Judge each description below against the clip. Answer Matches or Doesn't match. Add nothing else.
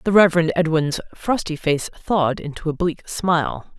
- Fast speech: Doesn't match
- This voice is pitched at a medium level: Matches